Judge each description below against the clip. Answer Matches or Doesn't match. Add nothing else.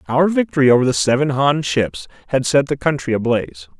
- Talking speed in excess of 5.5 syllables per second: Matches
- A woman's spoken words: Doesn't match